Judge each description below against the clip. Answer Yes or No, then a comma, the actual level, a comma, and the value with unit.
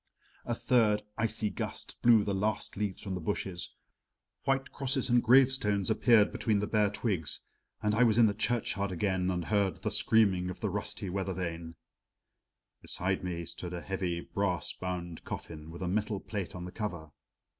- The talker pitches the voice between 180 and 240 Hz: No, low, 100 Hz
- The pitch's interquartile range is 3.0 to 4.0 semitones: Yes, average, 3.3 semitones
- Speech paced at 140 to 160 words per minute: No, average, 175 wpm